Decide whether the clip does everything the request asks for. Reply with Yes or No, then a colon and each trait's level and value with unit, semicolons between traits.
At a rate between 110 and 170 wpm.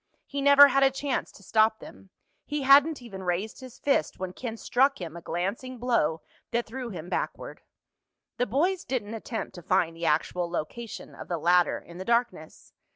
No: average, 185 wpm